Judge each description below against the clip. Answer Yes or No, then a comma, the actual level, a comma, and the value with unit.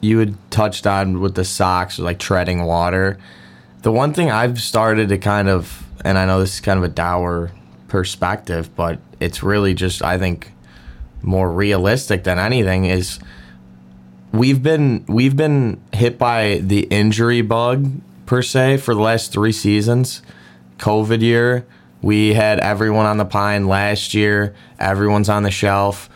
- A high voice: No, low, 100 Hz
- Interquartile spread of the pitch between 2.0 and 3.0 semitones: No, average, 3.7 semitones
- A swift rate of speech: No, average, 160 wpm